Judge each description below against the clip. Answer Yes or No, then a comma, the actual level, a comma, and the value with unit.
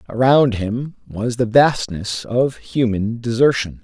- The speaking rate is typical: No, slow, 125 wpm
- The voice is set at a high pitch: No, low, 120 Hz